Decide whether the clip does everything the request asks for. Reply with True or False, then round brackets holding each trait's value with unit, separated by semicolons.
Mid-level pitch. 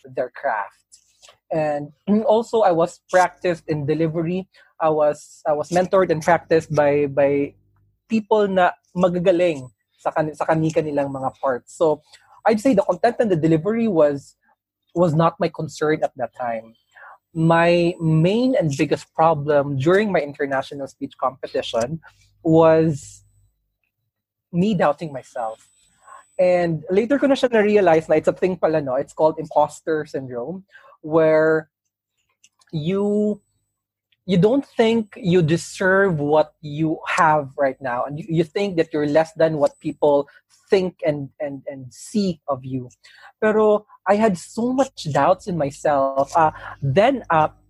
True (160 Hz)